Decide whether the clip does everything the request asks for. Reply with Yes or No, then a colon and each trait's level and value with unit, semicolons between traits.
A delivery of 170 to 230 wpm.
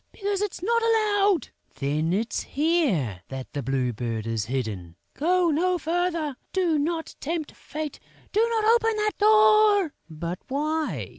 No: average, 145 wpm